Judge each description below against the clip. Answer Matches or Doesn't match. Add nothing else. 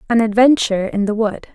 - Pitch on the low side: Doesn't match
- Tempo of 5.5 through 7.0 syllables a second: Matches